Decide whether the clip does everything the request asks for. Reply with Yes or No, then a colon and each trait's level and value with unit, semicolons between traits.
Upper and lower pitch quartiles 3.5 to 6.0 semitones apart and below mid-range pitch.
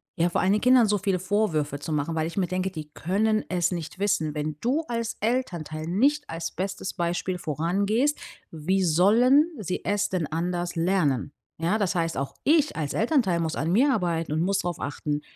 No: average, 4.4 semitones; medium, 180 Hz